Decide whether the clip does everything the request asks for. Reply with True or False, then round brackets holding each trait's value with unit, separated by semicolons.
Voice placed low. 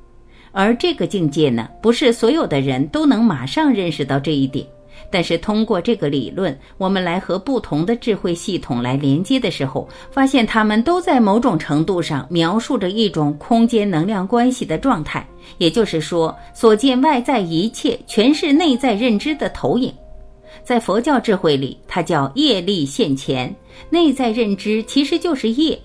False (200 Hz)